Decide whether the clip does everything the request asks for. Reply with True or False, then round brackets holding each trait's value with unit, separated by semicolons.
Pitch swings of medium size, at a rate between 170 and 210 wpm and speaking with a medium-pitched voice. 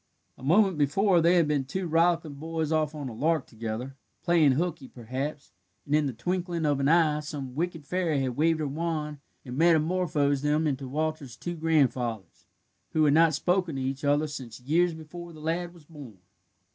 True (3.3 semitones; 185 wpm; 155 Hz)